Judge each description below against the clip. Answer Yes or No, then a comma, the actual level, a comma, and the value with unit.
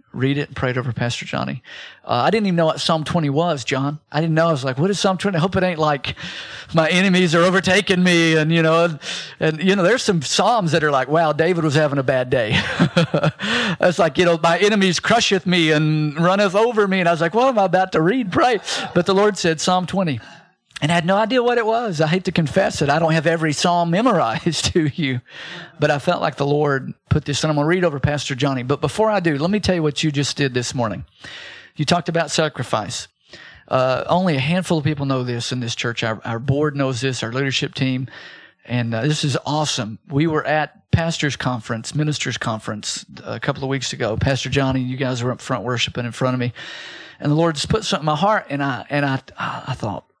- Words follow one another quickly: Yes, fast, 245 wpm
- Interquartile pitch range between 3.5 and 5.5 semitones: Yes, average, 4.5 semitones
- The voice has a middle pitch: Yes, medium, 155 Hz